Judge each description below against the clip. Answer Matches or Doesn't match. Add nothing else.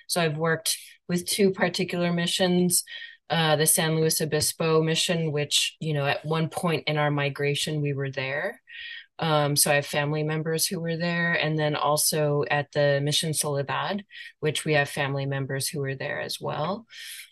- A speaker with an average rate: Matches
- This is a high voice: Doesn't match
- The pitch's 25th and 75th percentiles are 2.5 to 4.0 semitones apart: Matches